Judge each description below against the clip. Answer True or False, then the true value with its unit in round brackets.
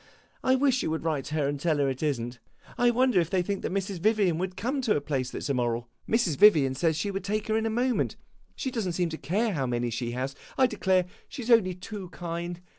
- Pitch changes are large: True (7.0 semitones)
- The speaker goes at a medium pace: False (265 wpm)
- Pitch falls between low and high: True (180 Hz)